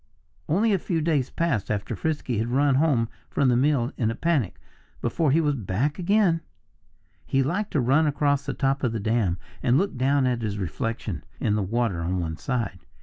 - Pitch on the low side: Yes, low, 130 Hz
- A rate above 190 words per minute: Yes, average, 200 wpm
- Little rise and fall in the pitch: No, average, 5.0 semitones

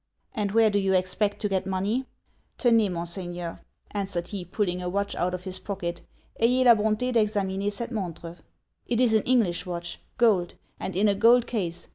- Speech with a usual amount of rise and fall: Yes, average, 3.5 semitones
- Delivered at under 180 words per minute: No, average, 185 wpm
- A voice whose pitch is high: Yes, high, 200 Hz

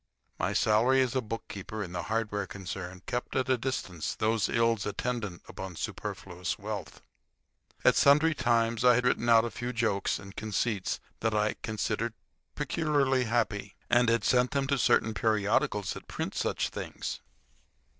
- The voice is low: Yes, low, 115 Hz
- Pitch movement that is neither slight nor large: Yes, average, 3.3 semitones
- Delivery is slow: No, average, 155 wpm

